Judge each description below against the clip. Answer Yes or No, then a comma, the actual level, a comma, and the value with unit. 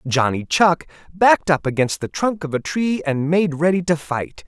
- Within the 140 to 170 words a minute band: No, average, 200 wpm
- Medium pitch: Yes, medium, 165 Hz